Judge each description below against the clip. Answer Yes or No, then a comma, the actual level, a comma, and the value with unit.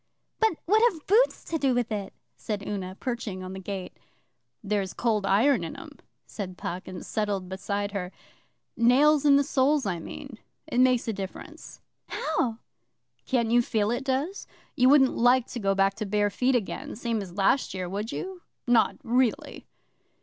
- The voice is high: Yes, high, 225 Hz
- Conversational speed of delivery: Yes, average, 175 wpm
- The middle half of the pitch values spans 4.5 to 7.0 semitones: Yes, average, 5.0 semitones